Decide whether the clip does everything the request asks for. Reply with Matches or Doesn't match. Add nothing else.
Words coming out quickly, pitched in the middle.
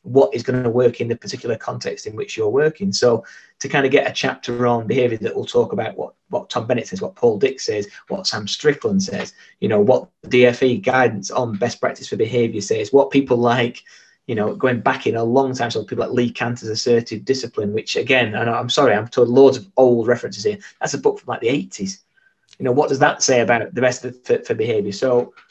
Doesn't match